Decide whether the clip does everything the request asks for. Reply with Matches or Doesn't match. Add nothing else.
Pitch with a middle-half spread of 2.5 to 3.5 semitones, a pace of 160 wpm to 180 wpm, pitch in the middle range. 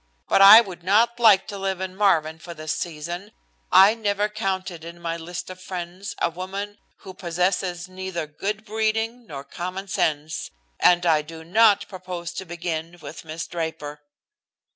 Matches